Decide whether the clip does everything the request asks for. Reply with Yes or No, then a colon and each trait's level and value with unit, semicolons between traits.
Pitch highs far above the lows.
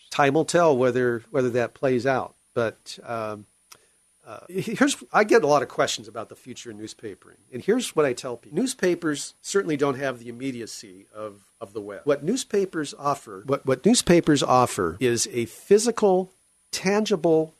Yes: wide, 7.5 semitones